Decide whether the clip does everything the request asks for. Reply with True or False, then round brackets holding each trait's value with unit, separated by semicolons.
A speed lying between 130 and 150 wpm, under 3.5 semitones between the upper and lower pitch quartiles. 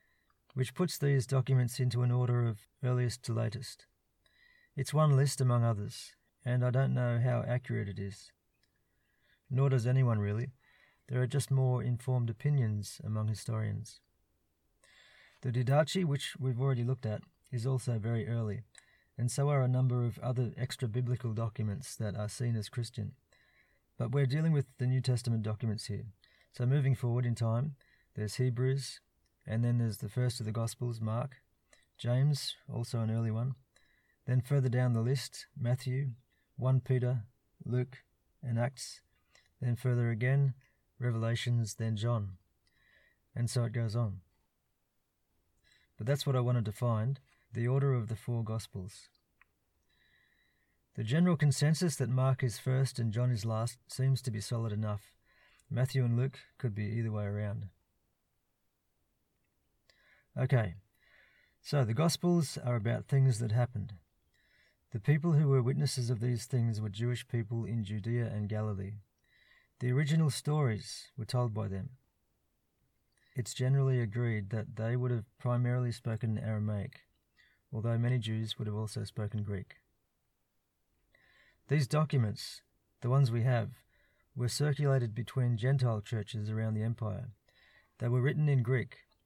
True (145 wpm; 2.8 semitones)